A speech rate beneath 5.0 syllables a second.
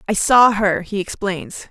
Yes: 4.0 syllables/s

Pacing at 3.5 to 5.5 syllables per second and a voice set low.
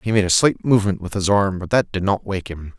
No: 5.9 syllables/s; low, 100 Hz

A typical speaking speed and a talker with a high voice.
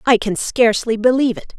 Yes: average, 190 wpm; high, 230 Hz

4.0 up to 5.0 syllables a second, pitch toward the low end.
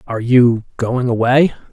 Yes: 4.6 syllables/s; low, 125 Hz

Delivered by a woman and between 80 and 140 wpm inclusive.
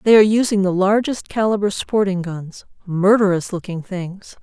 Yes: female; slow, 135 wpm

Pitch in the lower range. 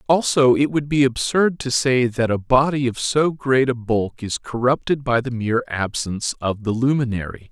Yes: low, 125 Hz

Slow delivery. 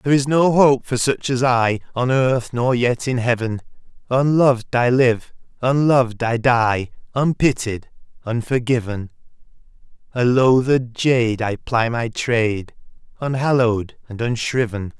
Yes: slow, 130 wpm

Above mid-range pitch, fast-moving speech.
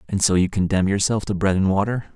No: low, 100 Hz; fast, 250 wpm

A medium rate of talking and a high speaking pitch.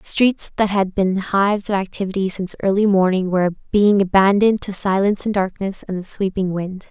Yes: average, 185 wpm; high, 195 Hz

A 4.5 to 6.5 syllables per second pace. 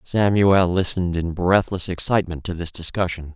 Yes: 5.2 syllables/s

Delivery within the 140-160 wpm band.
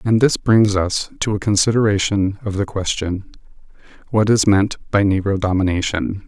Yes: average, 155 wpm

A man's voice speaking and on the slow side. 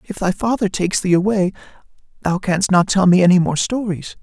No: male; average, 200 wpm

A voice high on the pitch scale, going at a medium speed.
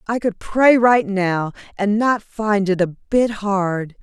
Yes: high, 205 Hz; average, 180 wpm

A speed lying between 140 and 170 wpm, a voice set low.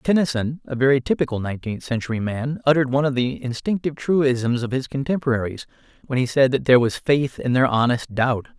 No: average, 190 wpm; low, 130 Hz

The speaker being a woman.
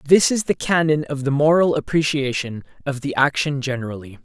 No: male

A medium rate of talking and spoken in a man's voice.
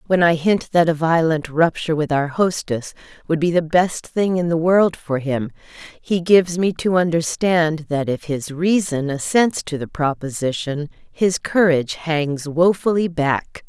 No: average, 165 wpm; female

